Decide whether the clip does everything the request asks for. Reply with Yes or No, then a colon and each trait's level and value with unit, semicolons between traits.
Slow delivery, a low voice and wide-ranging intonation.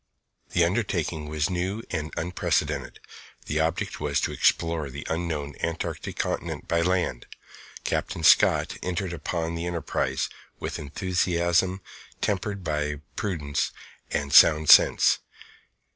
No: slow, 115 wpm; very low, 85 Hz; average, 2.9 semitones